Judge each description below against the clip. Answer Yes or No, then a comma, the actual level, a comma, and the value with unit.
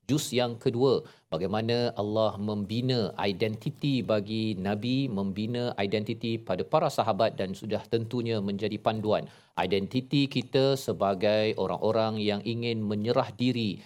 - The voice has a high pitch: No, low, 110 Hz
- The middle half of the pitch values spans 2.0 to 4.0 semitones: Yes, average, 2.9 semitones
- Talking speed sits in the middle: Yes, average, 115 wpm